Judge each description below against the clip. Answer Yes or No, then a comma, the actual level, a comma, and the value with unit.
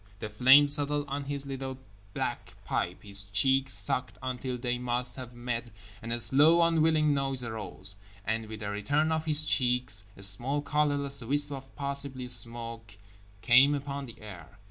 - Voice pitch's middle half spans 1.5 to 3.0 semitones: No, average, 3.7 semitones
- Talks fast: No, average, 165 wpm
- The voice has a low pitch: Yes, low, 130 Hz